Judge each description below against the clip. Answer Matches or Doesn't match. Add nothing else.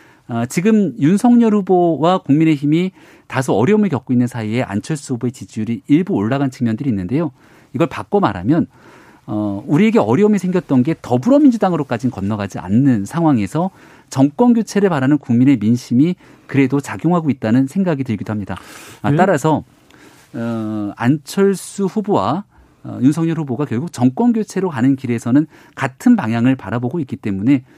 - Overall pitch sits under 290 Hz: Matches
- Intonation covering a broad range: Matches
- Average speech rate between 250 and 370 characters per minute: Matches